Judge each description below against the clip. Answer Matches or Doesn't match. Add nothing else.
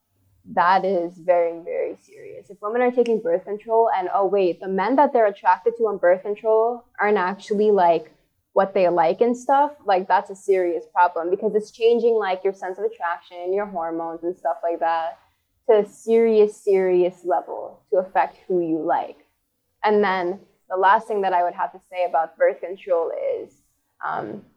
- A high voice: Matches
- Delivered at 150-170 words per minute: Doesn't match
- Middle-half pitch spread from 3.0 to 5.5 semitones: Matches